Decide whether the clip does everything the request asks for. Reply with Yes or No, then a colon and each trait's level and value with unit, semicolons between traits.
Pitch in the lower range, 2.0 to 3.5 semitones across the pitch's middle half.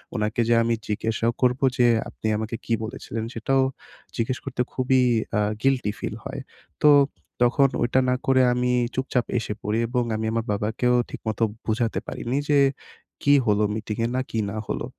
Yes: low, 120 Hz; average, 2.7 semitones